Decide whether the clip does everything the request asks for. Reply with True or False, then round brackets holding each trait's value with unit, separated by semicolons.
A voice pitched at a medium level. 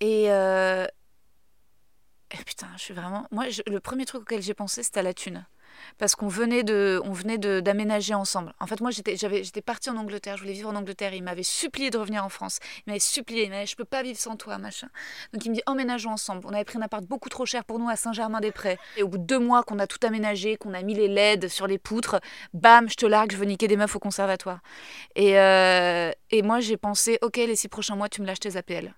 False (210 Hz)